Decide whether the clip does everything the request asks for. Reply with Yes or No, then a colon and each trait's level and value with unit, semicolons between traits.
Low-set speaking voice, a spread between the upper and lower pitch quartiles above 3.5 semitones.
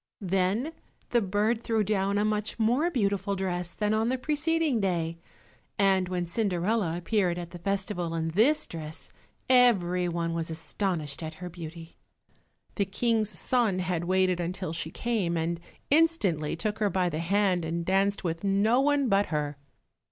No: high, 190 Hz; average, 4.0 semitones